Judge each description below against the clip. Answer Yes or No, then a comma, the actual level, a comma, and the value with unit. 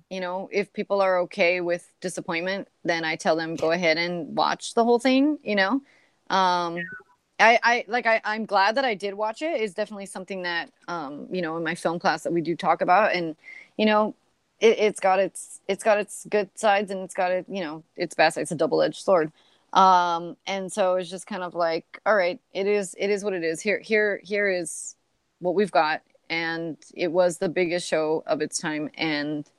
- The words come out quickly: Yes, fast, 220 wpm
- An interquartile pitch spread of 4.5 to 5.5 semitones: No, average, 3.5 semitones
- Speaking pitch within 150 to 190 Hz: Yes, medium, 185 Hz